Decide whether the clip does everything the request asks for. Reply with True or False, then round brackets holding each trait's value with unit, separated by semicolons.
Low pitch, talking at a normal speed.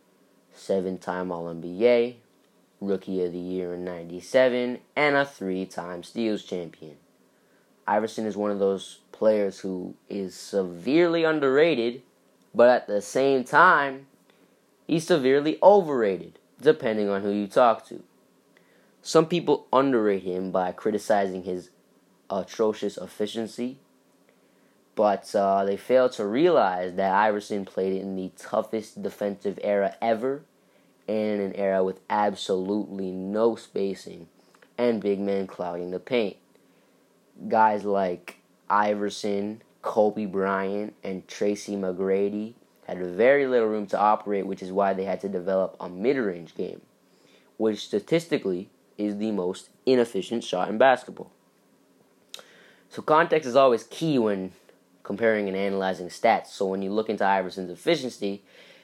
False (100 Hz; 125 wpm)